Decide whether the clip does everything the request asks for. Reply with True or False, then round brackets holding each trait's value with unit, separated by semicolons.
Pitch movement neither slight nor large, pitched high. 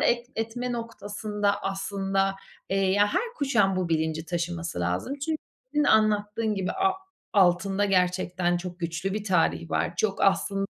True (3.4 semitones; 195 Hz)